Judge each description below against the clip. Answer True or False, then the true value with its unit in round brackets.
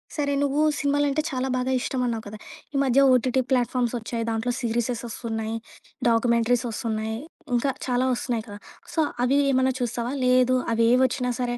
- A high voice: True (245 Hz)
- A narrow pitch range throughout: True (2.2 semitones)